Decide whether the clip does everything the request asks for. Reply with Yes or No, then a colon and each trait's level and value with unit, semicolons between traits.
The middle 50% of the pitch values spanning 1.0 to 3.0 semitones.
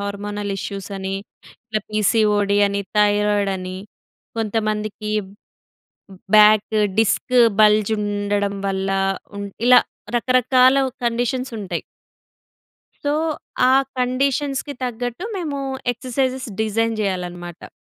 No: average, 3.6 semitones